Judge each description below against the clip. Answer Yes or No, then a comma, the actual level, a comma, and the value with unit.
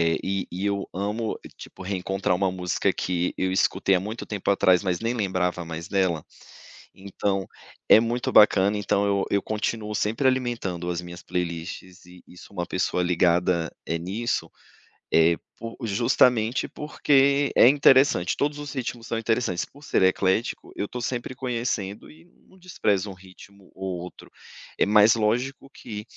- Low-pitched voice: Yes, low, 100 Hz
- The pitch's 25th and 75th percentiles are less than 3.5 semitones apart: No, average, 4.4 semitones